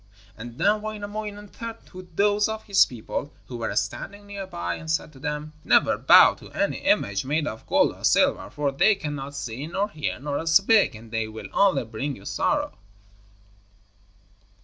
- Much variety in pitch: Yes, wide, 8.9 semitones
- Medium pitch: Yes, medium, 150 Hz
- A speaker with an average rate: Yes, average, 175 wpm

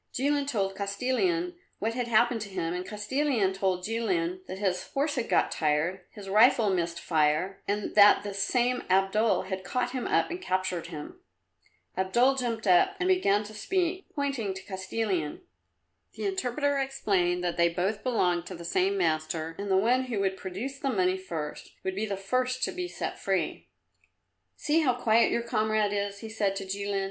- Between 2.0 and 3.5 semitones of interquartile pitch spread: No, average, 5.2 semitones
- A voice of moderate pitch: No, high, 205 Hz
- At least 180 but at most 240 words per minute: Yes, average, 185 wpm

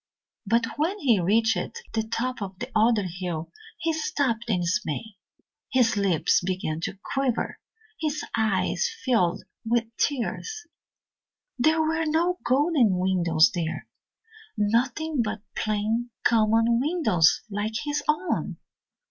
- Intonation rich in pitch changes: Yes, wide, 6.3 semitones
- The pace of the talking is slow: Yes, slow, 120 wpm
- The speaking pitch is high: Yes, high, 225 Hz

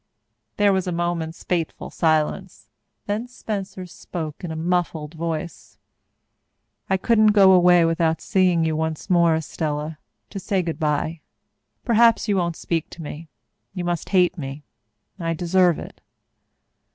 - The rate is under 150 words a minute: Yes, average, 140 wpm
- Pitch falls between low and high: Yes, medium, 170 Hz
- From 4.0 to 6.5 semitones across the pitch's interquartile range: No, average, 2.8 semitones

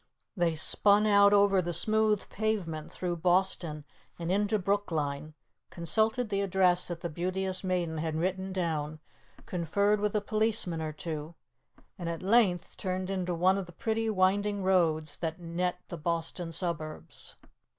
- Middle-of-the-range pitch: Yes, medium, 180 Hz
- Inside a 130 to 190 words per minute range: Yes, average, 150 wpm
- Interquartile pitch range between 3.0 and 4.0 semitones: Yes, average, 3.4 semitones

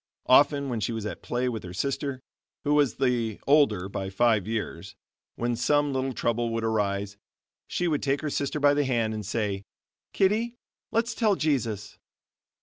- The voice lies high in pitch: No, low, 120 Hz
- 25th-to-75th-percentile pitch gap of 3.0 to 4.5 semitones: No, average, 4.9 semitones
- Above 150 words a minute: Yes, average, 170 wpm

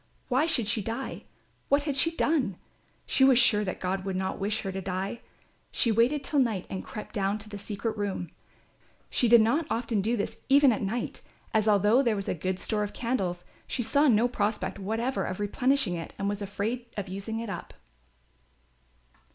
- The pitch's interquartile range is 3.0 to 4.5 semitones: Yes, average, 3.8 semitones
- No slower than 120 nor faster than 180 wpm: No, average, 195 wpm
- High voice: Yes, high, 215 Hz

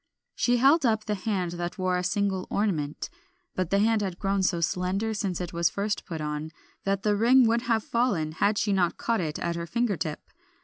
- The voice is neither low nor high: No, high, 195 Hz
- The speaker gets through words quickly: Yes, fast, 215 wpm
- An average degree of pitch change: Yes, average, 4.0 semitones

